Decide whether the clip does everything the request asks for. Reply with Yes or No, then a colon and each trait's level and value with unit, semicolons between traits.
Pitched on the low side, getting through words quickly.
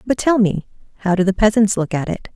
No: high, 200 Hz; fast, 255 wpm